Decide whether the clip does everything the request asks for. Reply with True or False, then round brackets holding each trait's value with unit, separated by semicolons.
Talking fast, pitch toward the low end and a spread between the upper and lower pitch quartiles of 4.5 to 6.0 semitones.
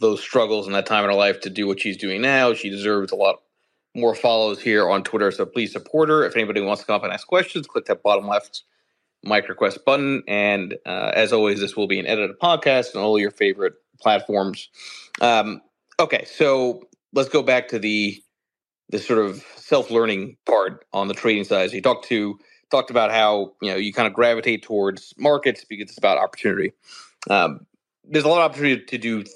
True (215 wpm; 110 Hz; 4.8 semitones)